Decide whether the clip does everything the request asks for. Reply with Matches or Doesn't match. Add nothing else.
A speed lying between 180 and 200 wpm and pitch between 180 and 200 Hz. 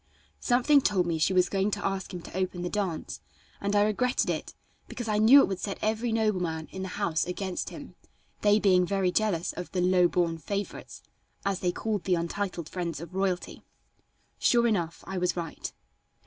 Matches